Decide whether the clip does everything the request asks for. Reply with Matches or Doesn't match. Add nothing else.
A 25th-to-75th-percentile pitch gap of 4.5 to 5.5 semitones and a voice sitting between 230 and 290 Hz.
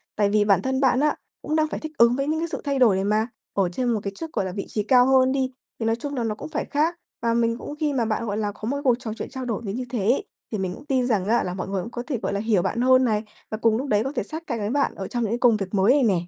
Doesn't match